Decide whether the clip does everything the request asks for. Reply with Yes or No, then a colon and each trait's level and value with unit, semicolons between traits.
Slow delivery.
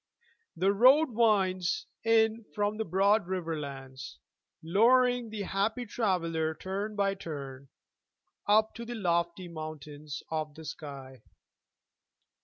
Yes: slow, 110 wpm